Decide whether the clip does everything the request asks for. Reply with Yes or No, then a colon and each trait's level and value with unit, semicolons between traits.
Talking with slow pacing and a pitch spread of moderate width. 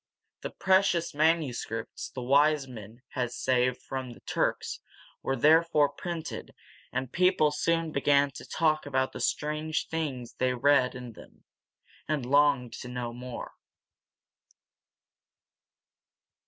Yes: slow, 120 wpm; average, 3.6 semitones